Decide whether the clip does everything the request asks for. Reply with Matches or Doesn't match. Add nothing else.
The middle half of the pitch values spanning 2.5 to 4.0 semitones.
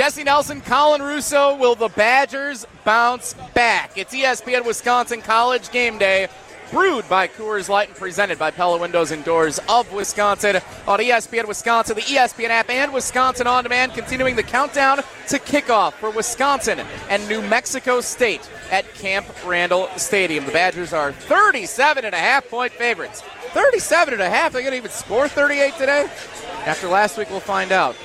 Doesn't match